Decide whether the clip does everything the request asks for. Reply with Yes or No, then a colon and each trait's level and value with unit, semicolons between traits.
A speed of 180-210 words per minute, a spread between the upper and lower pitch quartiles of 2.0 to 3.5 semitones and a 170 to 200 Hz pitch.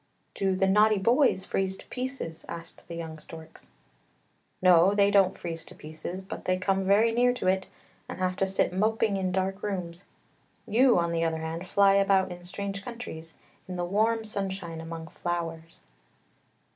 Yes: average, 185 wpm; average, 2.9 semitones; high, 190 Hz